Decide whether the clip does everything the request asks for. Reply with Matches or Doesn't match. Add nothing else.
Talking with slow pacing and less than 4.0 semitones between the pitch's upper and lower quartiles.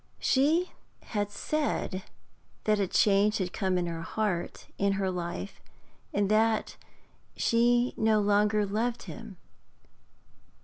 Matches